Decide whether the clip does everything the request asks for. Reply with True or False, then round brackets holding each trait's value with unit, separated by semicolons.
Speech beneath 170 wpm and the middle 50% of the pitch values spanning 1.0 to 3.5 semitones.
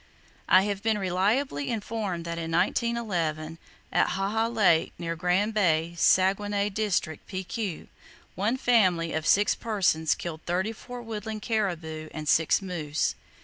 False (135 wpm; 4.4 semitones)